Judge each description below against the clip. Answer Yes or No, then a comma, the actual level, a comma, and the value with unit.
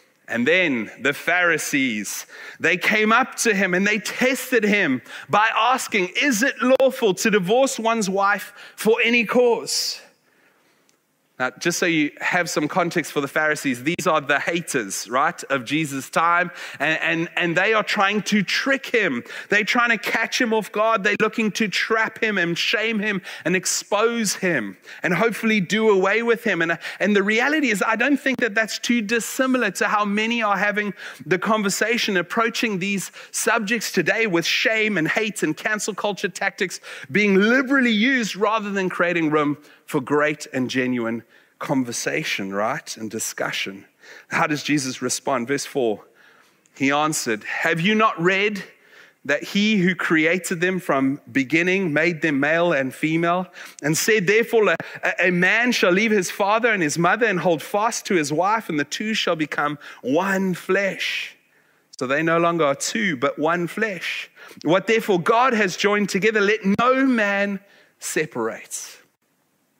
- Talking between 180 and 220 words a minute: No, average, 165 wpm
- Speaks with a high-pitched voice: Yes, high, 200 Hz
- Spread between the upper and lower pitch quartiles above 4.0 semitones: Yes, average, 5.1 semitones